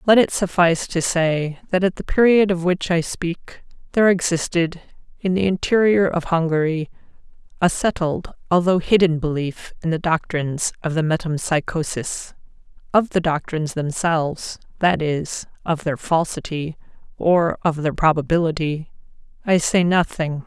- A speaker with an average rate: No, slow, 130 wpm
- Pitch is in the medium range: Yes, medium, 170 Hz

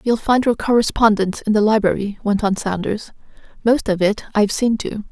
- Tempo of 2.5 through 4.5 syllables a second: No, 5.6 syllables/s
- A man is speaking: No, female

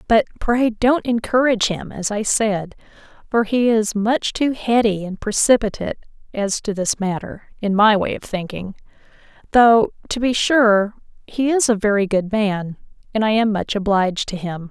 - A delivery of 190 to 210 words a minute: No, average, 170 wpm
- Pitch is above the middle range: Yes, high, 215 Hz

